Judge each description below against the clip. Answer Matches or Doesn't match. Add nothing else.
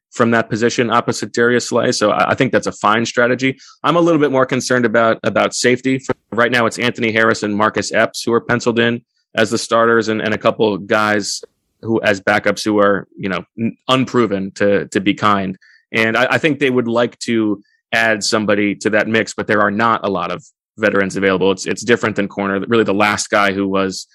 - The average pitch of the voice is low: Matches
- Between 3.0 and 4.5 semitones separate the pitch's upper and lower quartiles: Doesn't match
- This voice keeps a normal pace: Doesn't match